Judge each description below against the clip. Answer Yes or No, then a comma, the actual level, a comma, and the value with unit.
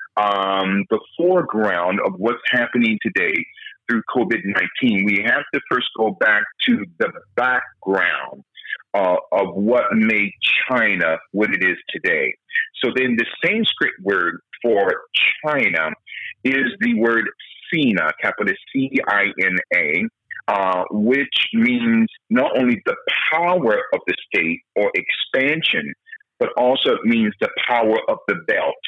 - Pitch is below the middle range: No, medium, 170 Hz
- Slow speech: Yes, slow, 125 wpm